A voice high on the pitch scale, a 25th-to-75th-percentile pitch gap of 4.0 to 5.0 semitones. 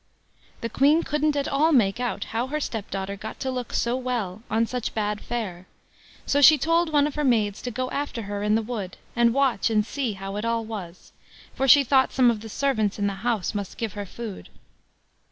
Yes: high, 230 Hz; average, 4.6 semitones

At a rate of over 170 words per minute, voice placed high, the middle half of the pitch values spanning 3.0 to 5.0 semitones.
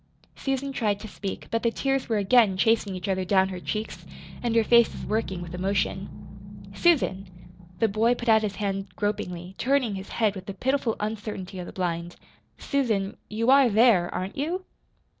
Yes: average, 180 wpm; high, 210 Hz; average, 3.7 semitones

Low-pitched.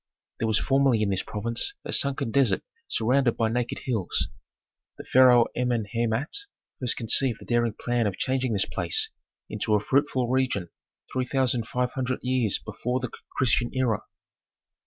Yes: low, 120 Hz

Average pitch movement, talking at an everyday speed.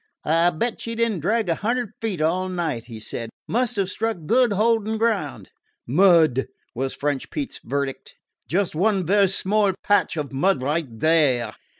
No: wide, 6.6 semitones; average, 175 wpm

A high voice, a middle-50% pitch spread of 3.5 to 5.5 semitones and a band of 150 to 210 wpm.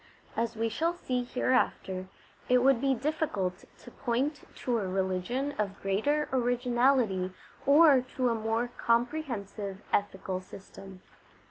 No: high, 235 Hz; average, 5.1 semitones; slow, 135 wpm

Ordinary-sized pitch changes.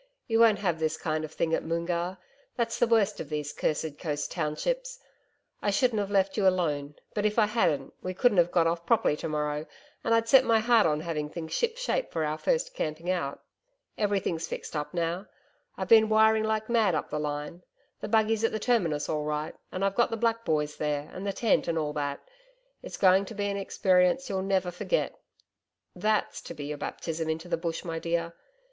No: wide, 5.7 semitones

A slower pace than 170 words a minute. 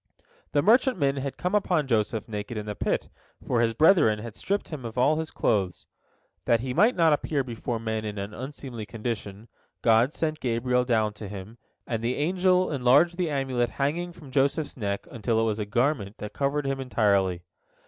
No: average, 190 wpm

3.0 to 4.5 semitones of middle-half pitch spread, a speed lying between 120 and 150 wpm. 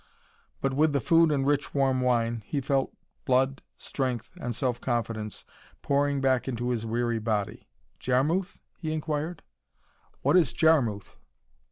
Yes: average, 3.6 semitones; average, 140 wpm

